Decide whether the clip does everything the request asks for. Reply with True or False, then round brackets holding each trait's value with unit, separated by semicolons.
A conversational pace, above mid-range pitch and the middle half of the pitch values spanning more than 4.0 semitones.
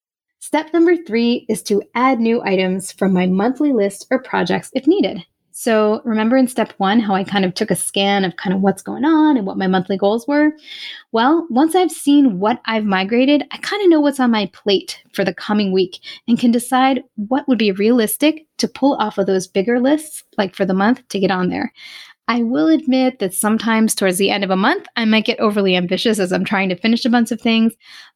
False (225 wpm; 230 Hz; 5.1 semitones)